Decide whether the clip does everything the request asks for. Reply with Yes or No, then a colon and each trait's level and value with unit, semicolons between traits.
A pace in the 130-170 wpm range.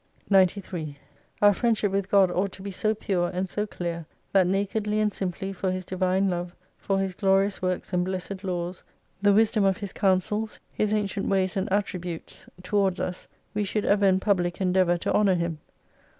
No: average, 185 wpm